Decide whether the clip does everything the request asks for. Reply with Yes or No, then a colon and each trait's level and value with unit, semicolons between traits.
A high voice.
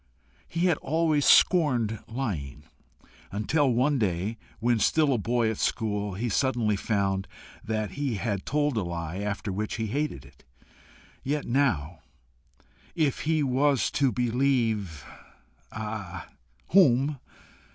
No: low, 115 Hz